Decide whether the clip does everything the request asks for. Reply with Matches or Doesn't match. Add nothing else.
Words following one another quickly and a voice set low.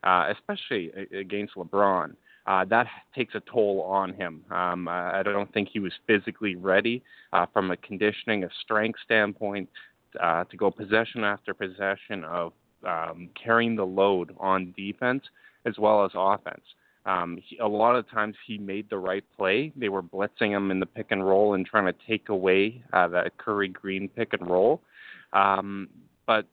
Doesn't match